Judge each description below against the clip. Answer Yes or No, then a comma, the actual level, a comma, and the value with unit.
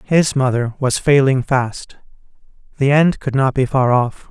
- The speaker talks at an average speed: Yes, average, 165 wpm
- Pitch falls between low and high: No, low, 130 Hz